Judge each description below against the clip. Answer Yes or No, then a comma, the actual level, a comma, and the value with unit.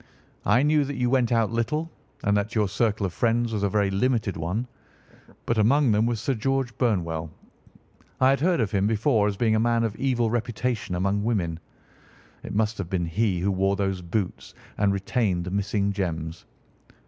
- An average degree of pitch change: Yes, average, 3.6 semitones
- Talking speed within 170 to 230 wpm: Yes, average, 190 wpm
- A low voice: Yes, low, 110 Hz